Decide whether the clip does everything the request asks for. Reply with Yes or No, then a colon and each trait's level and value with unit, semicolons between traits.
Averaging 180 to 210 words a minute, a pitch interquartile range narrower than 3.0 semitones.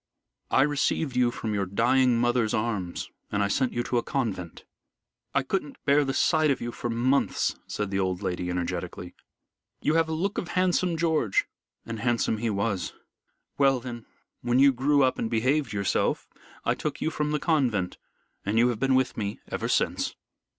No: average, 185 wpm; average, 4.8 semitones